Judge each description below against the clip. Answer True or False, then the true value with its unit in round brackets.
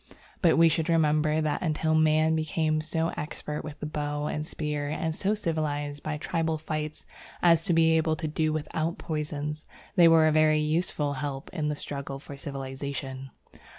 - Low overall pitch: False (155 Hz)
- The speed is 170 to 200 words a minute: True (175 wpm)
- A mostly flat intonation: True (1.4 semitones)